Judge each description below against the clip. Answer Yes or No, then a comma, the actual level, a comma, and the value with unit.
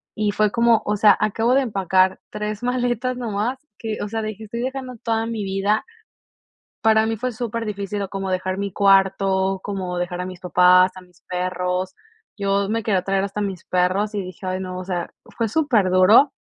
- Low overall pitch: No, high, 200 Hz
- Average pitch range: Yes, average, 3.1 semitones